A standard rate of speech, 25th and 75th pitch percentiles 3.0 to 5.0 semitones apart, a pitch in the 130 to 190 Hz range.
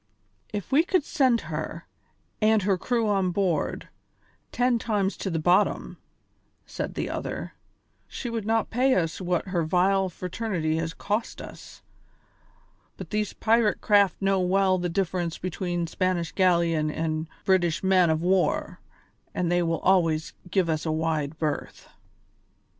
Yes: average, 150 wpm; average, 3.6 semitones; medium, 185 Hz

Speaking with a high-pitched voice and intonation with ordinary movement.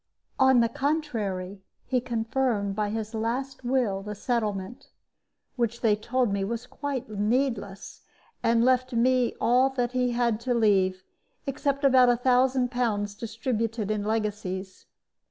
Yes: high, 235 Hz; average, 3.4 semitones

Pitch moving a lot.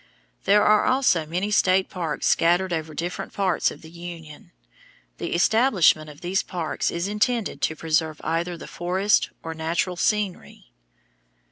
No: average, 3.2 semitones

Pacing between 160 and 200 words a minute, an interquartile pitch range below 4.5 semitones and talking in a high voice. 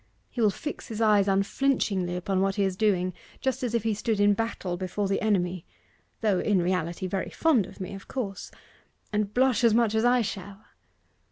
Yes: average, 195 wpm; average, 3.1 semitones; high, 205 Hz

